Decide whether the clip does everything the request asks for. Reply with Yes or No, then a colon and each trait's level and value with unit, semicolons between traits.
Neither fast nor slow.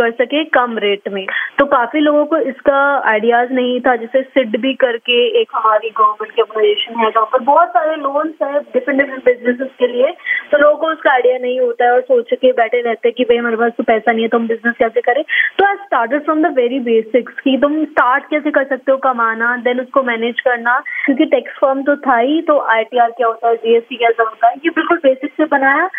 No: fast, 210 wpm